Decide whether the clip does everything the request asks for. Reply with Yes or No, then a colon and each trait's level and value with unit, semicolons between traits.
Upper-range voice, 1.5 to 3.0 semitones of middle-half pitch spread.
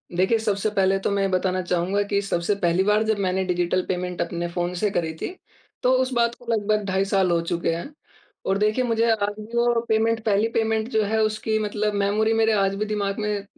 Yes: high, 205 Hz; average, 2.7 semitones